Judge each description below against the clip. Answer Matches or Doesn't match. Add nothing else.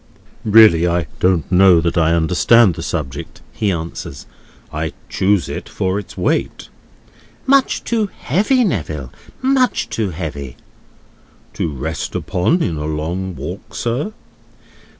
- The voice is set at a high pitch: Doesn't match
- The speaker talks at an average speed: Doesn't match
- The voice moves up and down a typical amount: Doesn't match